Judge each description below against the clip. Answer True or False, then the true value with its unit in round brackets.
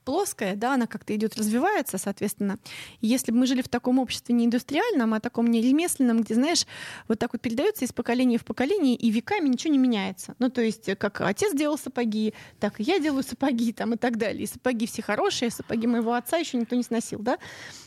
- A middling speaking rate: False (210 wpm)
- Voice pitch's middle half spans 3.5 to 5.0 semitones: False (2.4 semitones)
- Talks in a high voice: True (240 Hz)